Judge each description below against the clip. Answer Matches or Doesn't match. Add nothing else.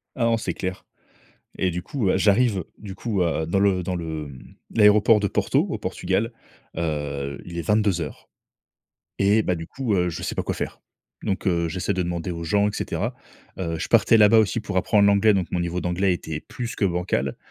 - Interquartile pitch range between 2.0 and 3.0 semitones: Doesn't match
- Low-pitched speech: Matches